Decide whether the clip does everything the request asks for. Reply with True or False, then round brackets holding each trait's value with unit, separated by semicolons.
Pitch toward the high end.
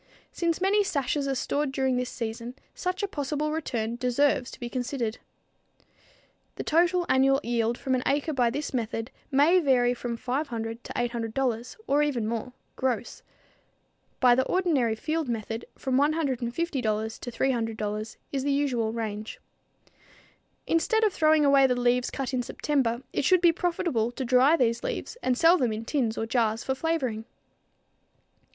True (255 Hz)